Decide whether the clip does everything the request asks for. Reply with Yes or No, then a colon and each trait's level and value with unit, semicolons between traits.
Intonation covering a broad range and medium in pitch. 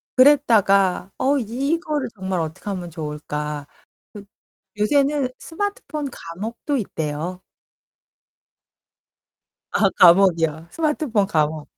No: wide, 8.9 semitones; high, 200 Hz